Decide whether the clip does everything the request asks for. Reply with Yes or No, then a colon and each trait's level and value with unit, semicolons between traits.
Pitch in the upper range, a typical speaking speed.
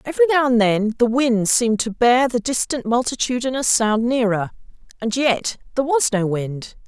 Yes: high, 240 Hz; average, 175 wpm